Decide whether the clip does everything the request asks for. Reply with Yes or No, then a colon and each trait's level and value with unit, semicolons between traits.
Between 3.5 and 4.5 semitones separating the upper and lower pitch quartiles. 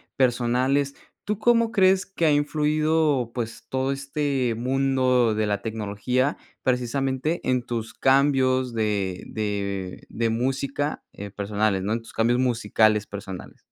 Yes: average, 4.1 semitones